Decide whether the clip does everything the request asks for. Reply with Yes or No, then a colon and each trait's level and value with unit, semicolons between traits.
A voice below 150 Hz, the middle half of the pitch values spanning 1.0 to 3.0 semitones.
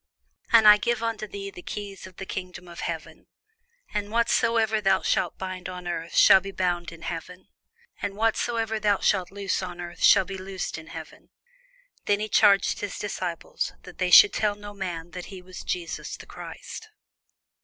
No: high, 190 Hz; narrow, 2.4 semitones